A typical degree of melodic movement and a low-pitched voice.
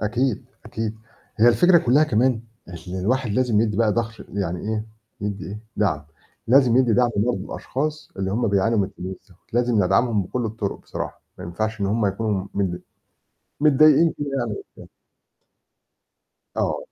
Yes: average, 3.7 semitones; low, 110 Hz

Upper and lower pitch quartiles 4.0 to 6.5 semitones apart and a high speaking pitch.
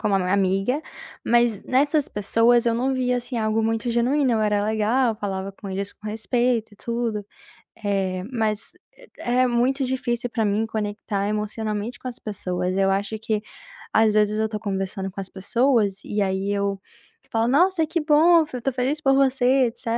No: average, 3.5 semitones; high, 220 Hz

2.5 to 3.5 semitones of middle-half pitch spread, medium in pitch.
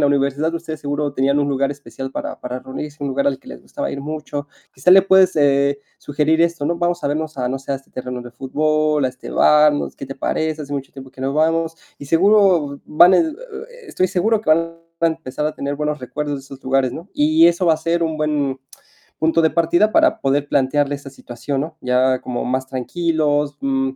Yes: average, 2.9 semitones; medium, 145 Hz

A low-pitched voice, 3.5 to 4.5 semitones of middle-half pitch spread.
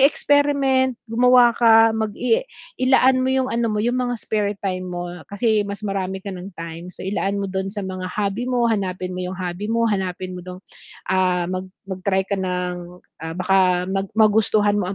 No: high, 200 Hz; average, 3.9 semitones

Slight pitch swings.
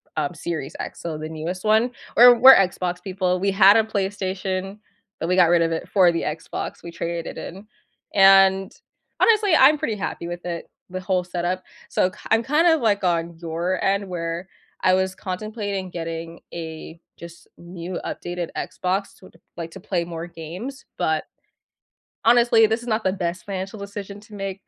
No: average, 3.0 semitones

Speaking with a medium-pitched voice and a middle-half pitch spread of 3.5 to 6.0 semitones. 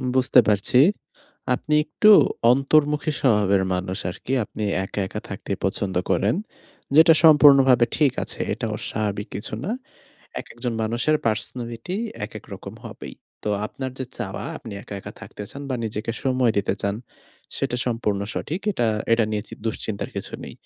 No: low, 115 Hz; average, 4.5 semitones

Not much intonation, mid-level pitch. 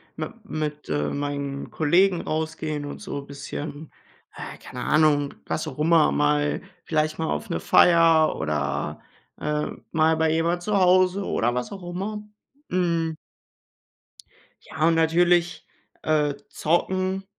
No: average, 3.1 semitones; medium, 160 Hz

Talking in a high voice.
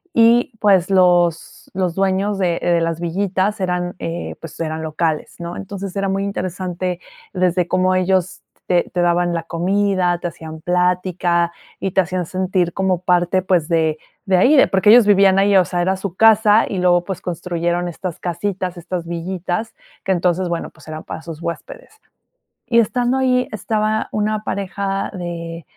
No: medium, 180 Hz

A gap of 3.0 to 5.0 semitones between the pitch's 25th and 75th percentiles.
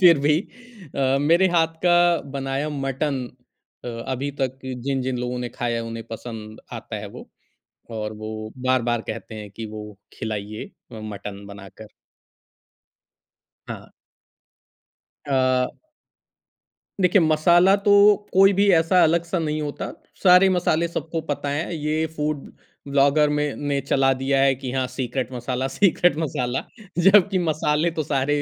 Yes: average, 4.6 semitones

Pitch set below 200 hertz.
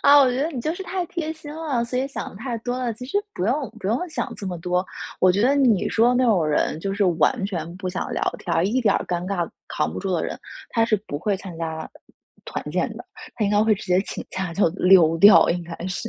No: high, 205 Hz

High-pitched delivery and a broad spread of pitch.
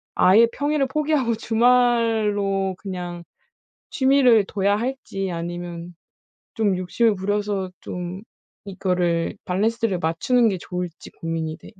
No: high, 200 Hz; average, 4.5 semitones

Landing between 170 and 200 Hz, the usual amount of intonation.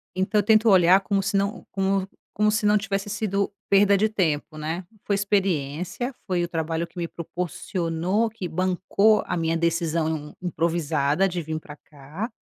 Yes: medium, 185 Hz; average, 3.5 semitones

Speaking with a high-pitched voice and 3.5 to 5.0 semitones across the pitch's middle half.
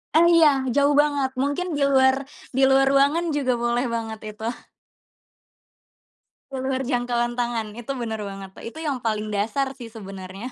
Yes: high, 245 Hz; average, 3.8 semitones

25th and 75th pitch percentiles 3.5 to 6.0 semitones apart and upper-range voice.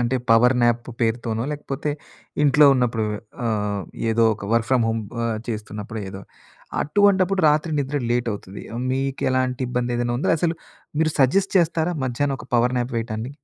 No: average, 4.1 semitones; low, 125 Hz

